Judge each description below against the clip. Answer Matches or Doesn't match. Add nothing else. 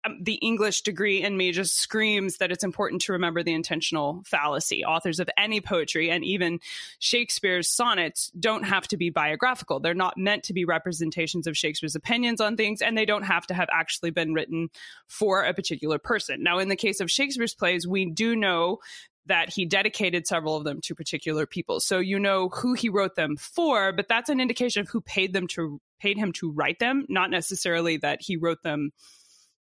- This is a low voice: Doesn't match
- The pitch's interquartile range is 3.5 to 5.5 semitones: Matches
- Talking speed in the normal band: Doesn't match